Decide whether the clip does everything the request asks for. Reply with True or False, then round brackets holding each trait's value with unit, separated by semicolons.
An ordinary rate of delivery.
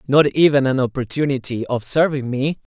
True (150 wpm)